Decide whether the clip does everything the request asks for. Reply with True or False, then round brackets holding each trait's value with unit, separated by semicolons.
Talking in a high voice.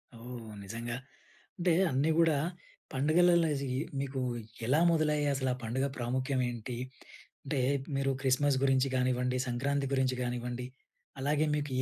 False (130 Hz)